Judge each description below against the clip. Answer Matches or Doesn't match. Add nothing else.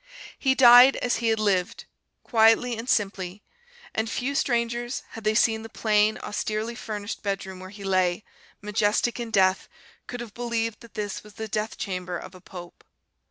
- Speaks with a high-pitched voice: Matches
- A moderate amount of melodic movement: Matches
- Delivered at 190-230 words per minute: Doesn't match